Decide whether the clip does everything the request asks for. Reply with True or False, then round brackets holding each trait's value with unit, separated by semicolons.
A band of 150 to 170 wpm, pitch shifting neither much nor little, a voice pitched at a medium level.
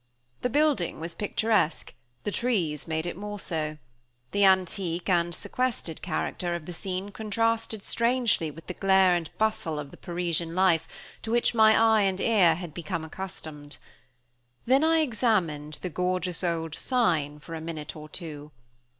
True (160 wpm; 5.0 semitones; 180 Hz)